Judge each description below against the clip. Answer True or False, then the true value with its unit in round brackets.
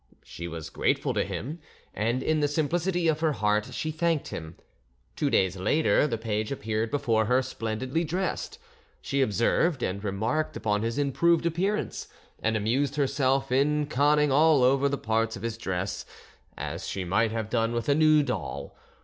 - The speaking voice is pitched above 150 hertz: False (130 Hz)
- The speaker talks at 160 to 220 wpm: True (170 wpm)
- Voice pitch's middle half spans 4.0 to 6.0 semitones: True (5.5 semitones)